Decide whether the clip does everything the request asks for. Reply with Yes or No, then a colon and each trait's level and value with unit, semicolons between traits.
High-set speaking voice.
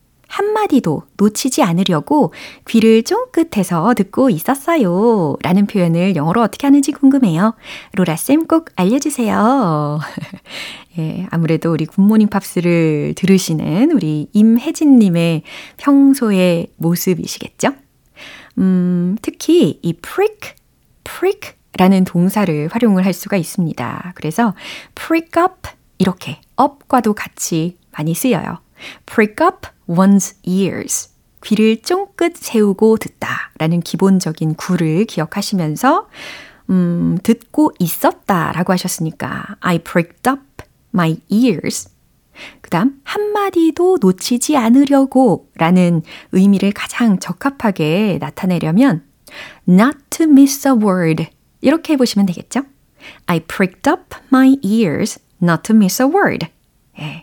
Yes: high, 205 Hz